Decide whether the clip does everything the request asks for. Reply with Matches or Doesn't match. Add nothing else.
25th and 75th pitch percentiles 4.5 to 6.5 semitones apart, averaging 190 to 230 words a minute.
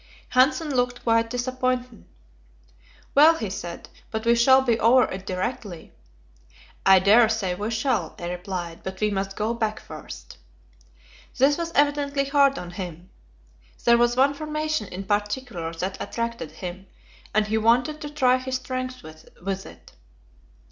Doesn't match